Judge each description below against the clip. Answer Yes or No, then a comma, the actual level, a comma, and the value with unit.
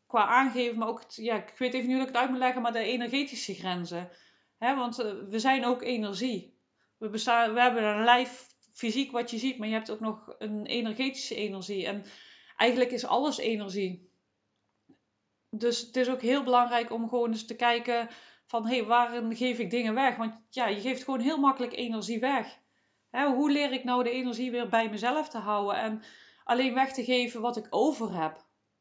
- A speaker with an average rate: No, fast, 205 wpm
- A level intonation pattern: Yes, narrow, 2.3 semitones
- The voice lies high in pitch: Yes, high, 240 Hz